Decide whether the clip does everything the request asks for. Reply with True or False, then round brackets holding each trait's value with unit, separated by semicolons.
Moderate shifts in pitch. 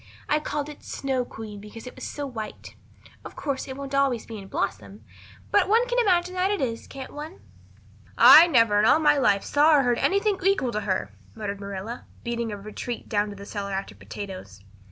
False (6.4 semitones)